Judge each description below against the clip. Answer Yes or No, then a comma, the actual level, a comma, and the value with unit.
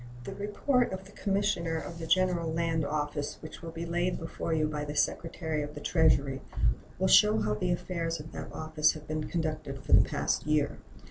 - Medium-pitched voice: Yes, medium, 160 Hz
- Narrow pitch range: Yes, narrow, 2.3 semitones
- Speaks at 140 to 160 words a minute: No, average, 200 wpm